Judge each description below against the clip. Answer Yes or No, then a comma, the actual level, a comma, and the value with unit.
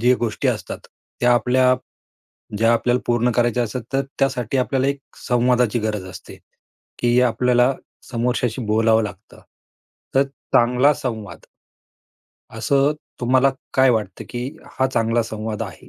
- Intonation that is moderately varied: No, narrow, 2.1 semitones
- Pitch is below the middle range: Yes, low, 120 Hz